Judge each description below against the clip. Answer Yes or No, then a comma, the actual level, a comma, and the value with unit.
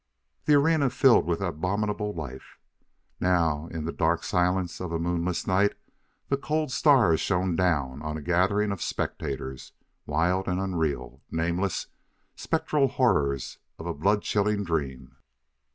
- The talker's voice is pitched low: Yes, very low, 90 Hz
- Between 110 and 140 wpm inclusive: Yes, slow, 135 wpm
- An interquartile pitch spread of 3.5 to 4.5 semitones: Yes, average, 4.1 semitones